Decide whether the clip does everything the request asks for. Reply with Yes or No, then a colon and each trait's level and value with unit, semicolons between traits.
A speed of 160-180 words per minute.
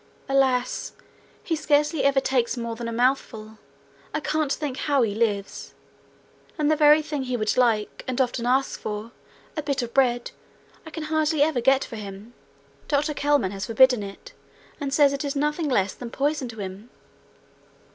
Yes: average, 175 wpm